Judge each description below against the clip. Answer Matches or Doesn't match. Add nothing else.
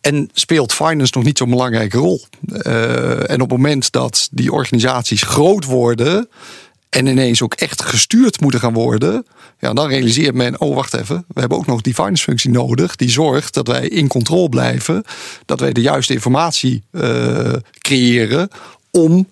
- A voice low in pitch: Matches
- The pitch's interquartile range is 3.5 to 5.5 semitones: Matches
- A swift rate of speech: Doesn't match